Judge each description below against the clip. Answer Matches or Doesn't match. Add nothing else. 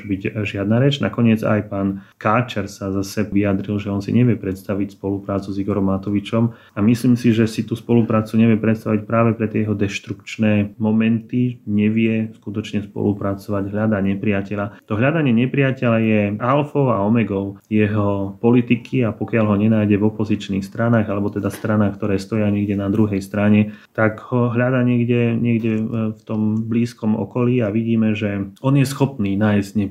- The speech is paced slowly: Doesn't match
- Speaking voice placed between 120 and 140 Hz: Doesn't match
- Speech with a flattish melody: Matches